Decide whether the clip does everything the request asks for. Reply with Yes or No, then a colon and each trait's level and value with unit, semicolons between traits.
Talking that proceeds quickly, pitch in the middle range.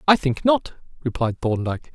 No: average, 155 wpm; medium, 145 Hz